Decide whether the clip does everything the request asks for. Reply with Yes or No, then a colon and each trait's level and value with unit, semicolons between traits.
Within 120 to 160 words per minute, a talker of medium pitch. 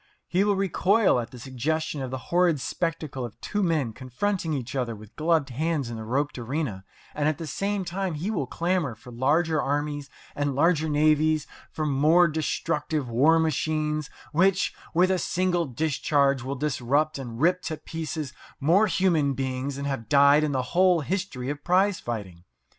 No: average, 175 wpm; medium, 150 Hz